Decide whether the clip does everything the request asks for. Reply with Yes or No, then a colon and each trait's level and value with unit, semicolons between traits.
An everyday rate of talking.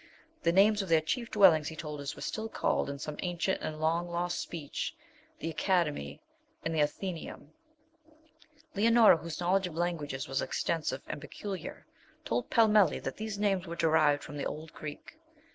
Yes: average, 170 wpm